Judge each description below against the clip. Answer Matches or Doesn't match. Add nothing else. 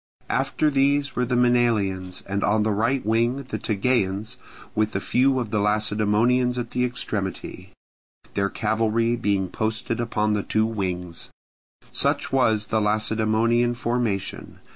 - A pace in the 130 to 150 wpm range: Matches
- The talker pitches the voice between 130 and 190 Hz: Doesn't match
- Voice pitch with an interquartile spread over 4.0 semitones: Doesn't match